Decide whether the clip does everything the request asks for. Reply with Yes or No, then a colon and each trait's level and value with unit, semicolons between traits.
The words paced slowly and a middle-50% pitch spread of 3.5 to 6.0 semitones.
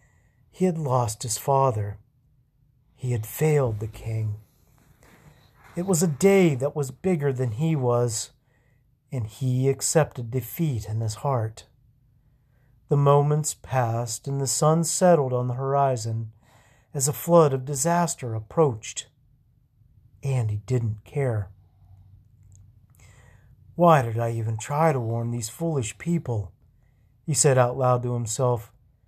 Yes: slow, 130 wpm; average, 3.9 semitones